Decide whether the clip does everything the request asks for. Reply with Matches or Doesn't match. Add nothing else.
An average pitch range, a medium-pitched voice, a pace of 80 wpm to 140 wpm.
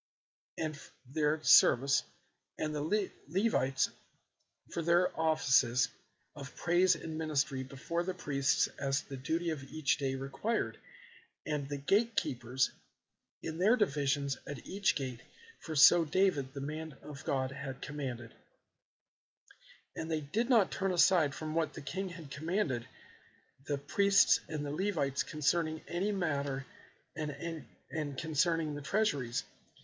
Matches